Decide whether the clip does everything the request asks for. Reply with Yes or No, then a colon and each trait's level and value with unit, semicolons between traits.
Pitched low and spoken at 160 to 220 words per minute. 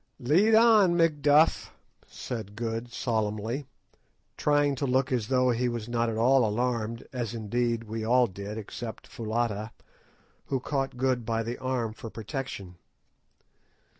No: low, 120 Hz; slow, 135 wpm